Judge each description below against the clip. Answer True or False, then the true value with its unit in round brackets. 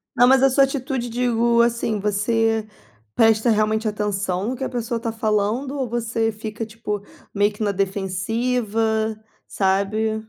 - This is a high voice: True (225 Hz)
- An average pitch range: False (2.2 semitones)